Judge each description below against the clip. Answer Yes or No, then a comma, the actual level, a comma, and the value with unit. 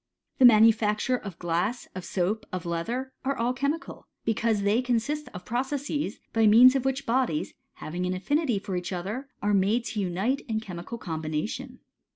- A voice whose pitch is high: Yes, high, 225 Hz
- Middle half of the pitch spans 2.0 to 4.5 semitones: No, wide, 5.6 semitones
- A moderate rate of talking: Yes, average, 170 wpm